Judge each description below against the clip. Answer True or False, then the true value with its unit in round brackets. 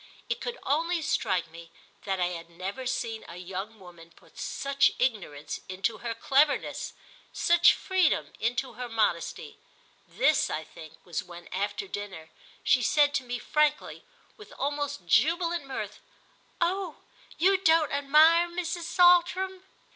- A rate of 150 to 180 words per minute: False (140 wpm)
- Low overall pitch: False (260 Hz)